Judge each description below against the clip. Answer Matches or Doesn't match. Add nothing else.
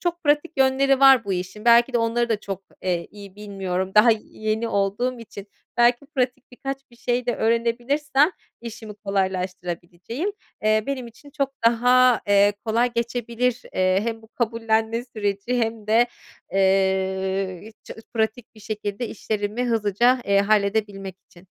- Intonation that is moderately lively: Matches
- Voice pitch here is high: Matches